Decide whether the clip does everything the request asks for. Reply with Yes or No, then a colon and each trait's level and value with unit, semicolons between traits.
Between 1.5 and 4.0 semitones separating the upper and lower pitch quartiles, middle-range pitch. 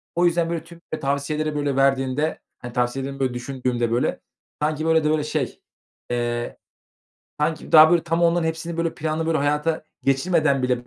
Yes: average, 3.4 semitones; medium, 150 Hz